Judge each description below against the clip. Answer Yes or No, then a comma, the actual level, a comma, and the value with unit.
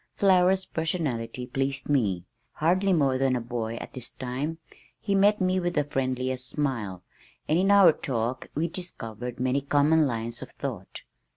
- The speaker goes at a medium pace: Yes, average, 160 wpm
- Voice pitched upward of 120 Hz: Yes, low, 135 Hz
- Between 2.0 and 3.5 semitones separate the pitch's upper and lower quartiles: No, average, 5.3 semitones